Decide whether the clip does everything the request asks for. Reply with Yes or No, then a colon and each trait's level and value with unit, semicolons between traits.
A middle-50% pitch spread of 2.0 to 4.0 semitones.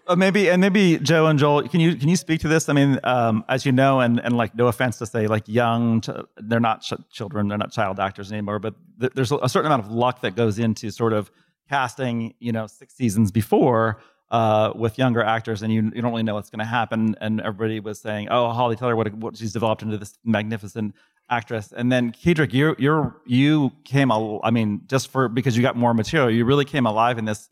Yes: average, 3.1 semitones